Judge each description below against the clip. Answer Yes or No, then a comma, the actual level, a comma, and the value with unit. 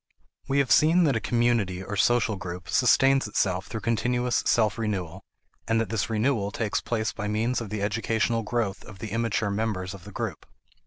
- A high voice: No, low, 110 Hz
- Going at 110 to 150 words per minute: No, average, 190 wpm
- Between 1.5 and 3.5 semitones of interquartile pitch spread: Yes, average, 2.8 semitones